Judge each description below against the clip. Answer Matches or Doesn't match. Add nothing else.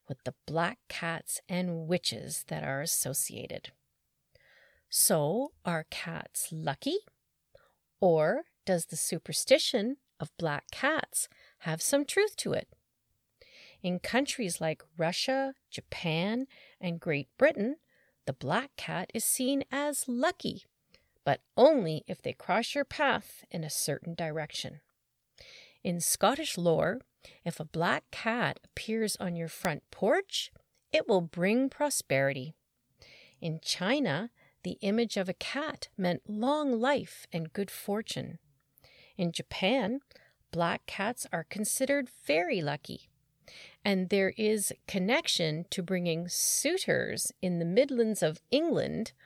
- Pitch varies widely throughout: Matches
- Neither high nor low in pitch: Doesn't match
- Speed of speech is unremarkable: Doesn't match